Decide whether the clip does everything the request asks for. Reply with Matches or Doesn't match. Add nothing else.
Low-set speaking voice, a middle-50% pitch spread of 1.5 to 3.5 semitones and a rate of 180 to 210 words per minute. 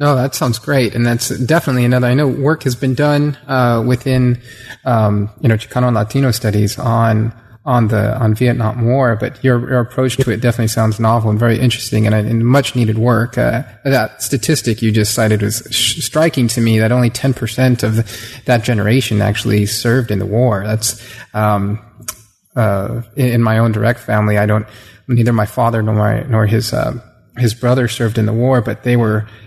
Matches